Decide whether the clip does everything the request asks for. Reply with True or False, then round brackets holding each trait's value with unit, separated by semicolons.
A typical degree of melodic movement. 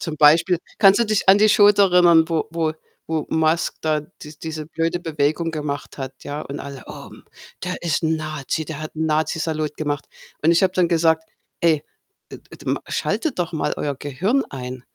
False (2.2 semitones)